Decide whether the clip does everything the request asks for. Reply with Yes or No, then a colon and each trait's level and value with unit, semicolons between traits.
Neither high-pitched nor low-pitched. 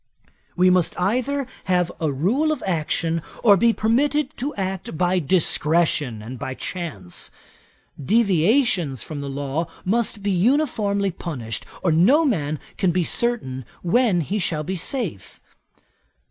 Yes: medium, 180 Hz